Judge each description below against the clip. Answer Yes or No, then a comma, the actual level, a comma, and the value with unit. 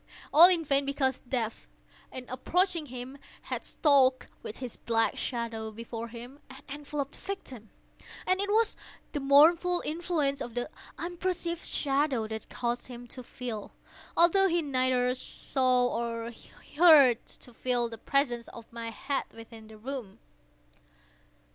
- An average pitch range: Yes, average, 4.3 semitones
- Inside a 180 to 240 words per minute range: No, slow, 135 wpm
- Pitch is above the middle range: Yes, very high, 260 Hz